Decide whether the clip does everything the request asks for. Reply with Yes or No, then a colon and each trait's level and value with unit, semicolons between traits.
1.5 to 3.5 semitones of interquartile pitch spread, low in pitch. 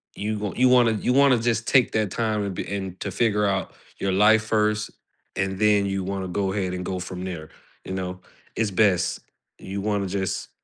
Yes: narrow, 2.4 semitones; low, 100 Hz